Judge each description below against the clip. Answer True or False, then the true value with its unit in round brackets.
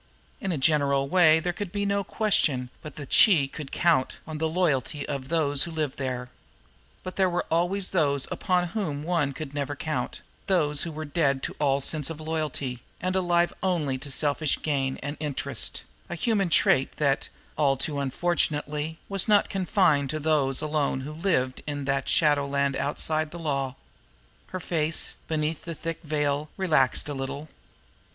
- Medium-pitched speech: True (150 Hz)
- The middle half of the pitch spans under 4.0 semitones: True (3.4 semitones)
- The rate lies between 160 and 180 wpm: True (170 wpm)